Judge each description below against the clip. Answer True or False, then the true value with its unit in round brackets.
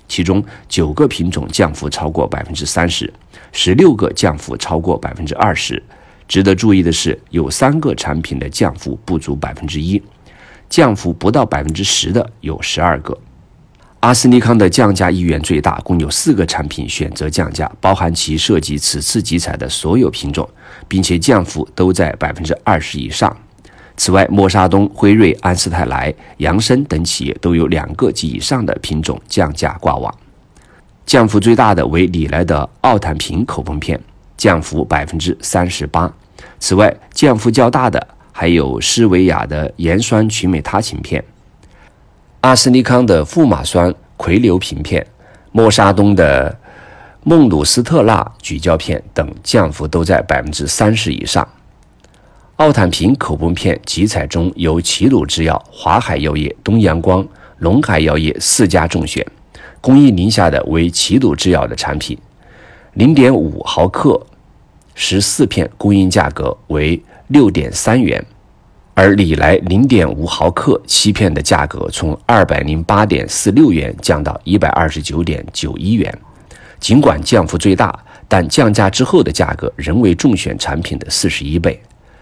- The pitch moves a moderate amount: True (4.8 semitones)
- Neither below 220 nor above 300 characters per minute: True (225 characters per minute)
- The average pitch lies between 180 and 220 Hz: False (90 Hz)